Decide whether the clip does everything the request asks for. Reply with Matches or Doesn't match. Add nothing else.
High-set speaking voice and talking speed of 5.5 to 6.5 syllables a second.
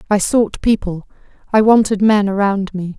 Doesn't match